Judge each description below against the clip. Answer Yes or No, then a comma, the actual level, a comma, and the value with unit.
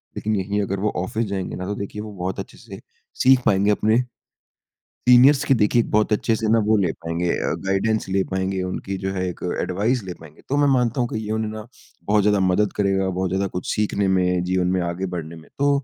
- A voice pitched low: Yes, low, 100 Hz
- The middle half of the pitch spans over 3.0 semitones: No, average, 2.7 semitones